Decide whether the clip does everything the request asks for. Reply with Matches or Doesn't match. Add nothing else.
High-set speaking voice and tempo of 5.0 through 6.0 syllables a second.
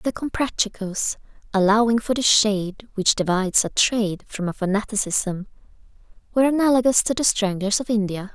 Matches